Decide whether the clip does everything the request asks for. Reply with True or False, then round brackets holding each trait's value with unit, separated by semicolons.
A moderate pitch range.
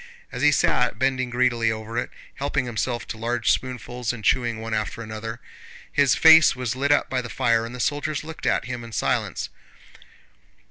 False (2.3 semitones)